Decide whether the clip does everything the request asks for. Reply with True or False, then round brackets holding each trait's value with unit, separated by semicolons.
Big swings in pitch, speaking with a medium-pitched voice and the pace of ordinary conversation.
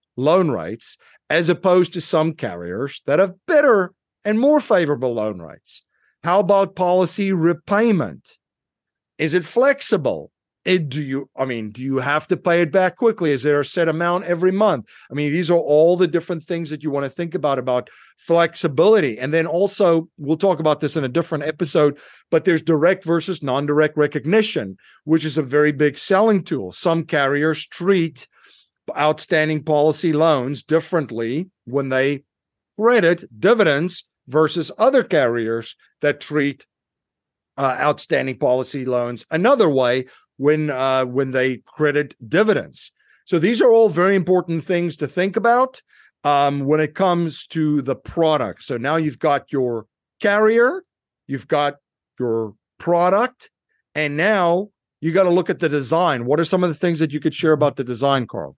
False (4.1 semitones; 155 Hz; 165 wpm)